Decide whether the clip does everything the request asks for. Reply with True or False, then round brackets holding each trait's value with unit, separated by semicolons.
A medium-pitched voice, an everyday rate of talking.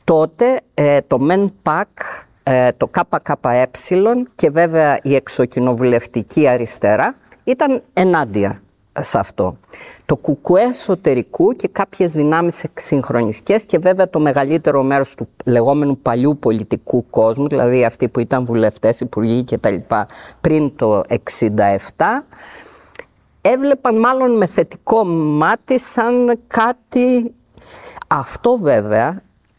False (150 Hz; 105 wpm)